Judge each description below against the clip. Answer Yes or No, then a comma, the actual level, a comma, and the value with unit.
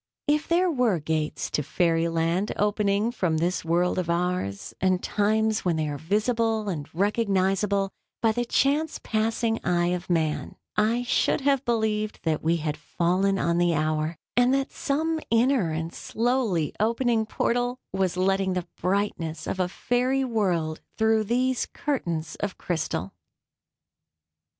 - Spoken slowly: No, average, 145 wpm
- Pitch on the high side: Yes, high, 195 Hz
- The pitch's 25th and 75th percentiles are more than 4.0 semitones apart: Yes, wide, 5.4 semitones